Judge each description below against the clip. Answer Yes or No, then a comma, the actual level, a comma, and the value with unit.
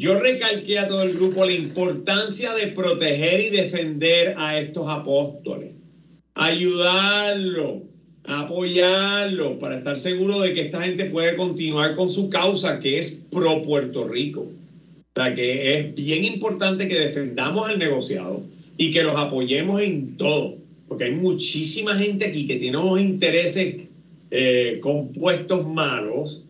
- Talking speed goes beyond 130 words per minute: Yes, average, 140 wpm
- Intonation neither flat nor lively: Yes, average, 3.6 semitones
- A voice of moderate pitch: Yes, medium, 170 Hz